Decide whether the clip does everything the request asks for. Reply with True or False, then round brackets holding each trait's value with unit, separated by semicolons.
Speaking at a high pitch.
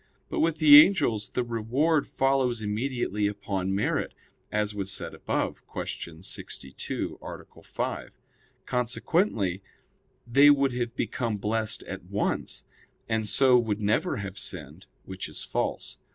False (110 Hz)